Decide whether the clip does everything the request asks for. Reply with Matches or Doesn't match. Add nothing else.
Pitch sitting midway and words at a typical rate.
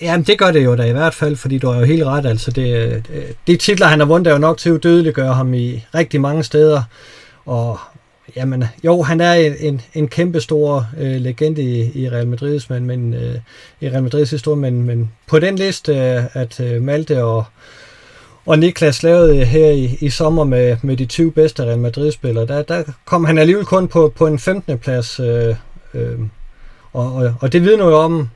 Matches